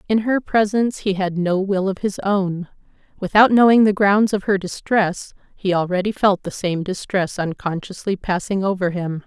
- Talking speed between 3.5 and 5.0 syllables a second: Yes, 4.8 syllables/s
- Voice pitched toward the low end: No, high, 195 Hz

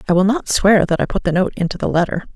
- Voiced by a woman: Yes, female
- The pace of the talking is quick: Yes, fast, 305 wpm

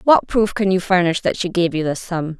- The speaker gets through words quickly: Yes, fast, 275 wpm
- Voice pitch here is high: No, medium, 180 Hz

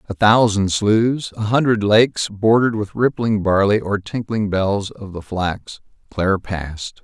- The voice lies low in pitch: Yes, low, 105 Hz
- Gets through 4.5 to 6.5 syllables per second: No, 4.3 syllables/s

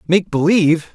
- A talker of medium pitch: Yes, medium, 170 Hz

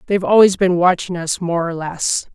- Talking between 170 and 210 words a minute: Yes, fast, 205 wpm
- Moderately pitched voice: Yes, medium, 175 Hz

